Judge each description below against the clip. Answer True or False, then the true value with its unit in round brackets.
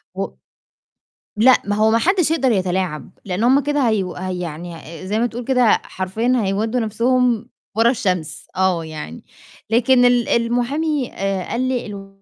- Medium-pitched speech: False (225 Hz)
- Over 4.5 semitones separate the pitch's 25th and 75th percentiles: True (4.9 semitones)